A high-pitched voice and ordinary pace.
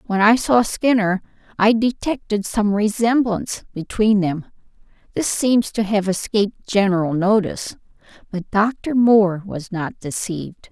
No: high, 210 Hz; slow, 125 wpm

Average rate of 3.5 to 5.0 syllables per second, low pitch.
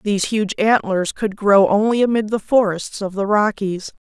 No: 4.6 syllables/s; high, 210 Hz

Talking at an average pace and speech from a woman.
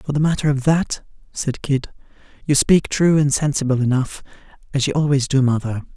No: average, 180 wpm; male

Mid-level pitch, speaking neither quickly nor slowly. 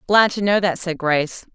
No: medium, 180 Hz; fast, 230 wpm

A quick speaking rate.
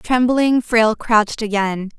No: slow, 120 wpm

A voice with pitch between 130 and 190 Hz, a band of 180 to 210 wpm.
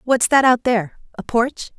No: high, 240 Hz; average, 200 wpm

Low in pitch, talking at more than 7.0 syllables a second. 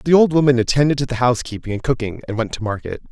Yes: low, 125 Hz; 7.5 syllables/s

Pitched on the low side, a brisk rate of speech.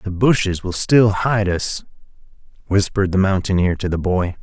No: very low, 95 Hz; average, 165 wpm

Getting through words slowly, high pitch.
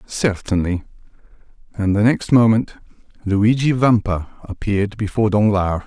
No: slow, 100 wpm; low, 105 Hz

